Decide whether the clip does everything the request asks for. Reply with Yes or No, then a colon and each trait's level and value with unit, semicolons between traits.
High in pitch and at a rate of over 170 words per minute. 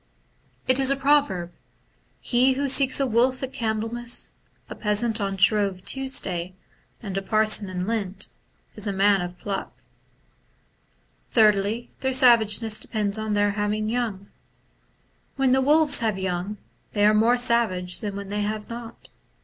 No: high, 215 Hz; average, 155 wpm